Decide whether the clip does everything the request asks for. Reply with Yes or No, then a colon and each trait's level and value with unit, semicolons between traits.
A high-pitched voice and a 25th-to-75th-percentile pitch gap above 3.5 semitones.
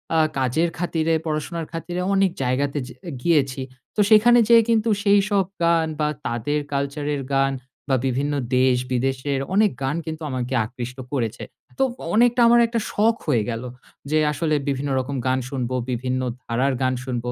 No: medium, 145 Hz; average, 5.1 semitones